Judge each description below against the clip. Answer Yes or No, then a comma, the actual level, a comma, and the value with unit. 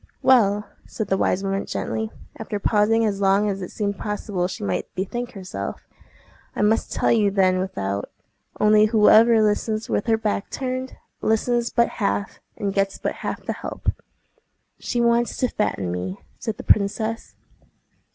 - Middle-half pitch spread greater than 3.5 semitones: No, narrow, 2.5 semitones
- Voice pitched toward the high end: Yes, high, 210 Hz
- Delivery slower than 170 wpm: Yes, average, 160 wpm